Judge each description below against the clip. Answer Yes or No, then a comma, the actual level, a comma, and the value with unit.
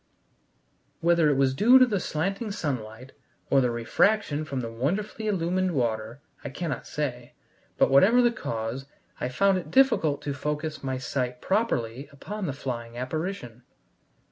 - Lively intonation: Yes, wide, 7.1 semitones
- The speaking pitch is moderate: Yes, medium, 145 Hz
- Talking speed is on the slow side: No, average, 150 wpm